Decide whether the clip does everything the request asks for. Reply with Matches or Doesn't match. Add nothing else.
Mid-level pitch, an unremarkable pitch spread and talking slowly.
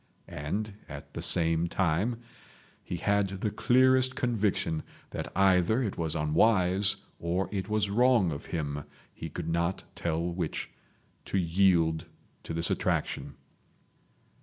Doesn't match